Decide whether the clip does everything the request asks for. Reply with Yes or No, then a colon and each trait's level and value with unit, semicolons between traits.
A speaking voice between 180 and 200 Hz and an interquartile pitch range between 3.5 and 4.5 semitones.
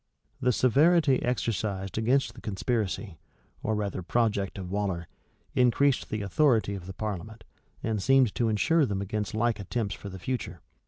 No: low, 110 Hz; average, 4.1 semitones